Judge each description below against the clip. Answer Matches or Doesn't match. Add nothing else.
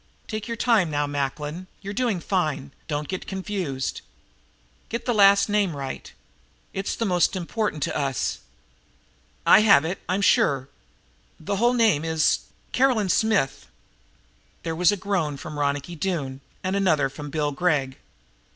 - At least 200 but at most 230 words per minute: Doesn't match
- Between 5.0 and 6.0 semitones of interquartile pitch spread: Matches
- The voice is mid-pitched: Matches